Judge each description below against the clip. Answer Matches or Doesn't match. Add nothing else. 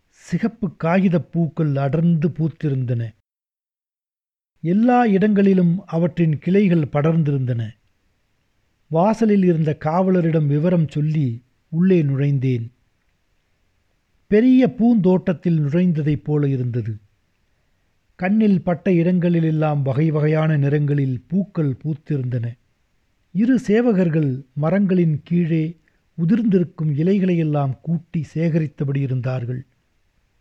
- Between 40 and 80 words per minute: Matches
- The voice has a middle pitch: Matches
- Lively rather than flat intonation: Matches